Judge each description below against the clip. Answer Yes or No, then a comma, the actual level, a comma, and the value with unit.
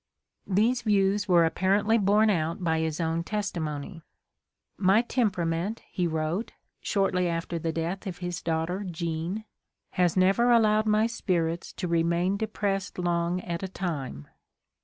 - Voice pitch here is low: No, medium, 180 Hz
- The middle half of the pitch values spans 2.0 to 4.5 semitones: Yes, average, 3.5 semitones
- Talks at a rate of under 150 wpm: Yes, average, 140 wpm